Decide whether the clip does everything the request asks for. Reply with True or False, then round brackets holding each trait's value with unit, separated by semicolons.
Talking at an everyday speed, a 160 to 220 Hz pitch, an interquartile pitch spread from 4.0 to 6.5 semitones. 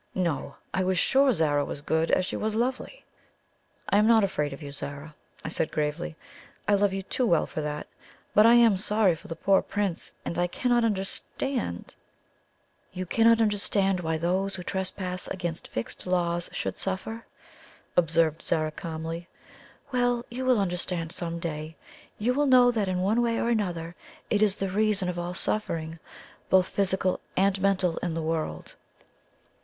True (170 wpm; 185 Hz; 4.3 semitones)